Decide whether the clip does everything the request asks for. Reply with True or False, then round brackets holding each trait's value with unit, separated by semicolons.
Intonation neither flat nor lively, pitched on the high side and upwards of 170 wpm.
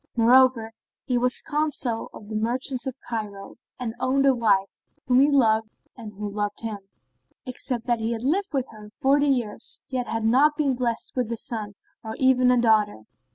True (3.0 semitones; 240 Hz; 185 wpm)